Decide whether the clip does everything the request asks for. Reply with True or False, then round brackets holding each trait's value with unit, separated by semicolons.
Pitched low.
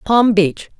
False (200 Hz)